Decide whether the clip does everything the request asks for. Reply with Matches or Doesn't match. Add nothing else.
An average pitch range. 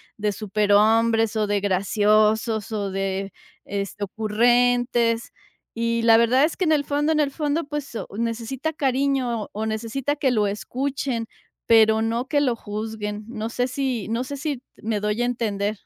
Matches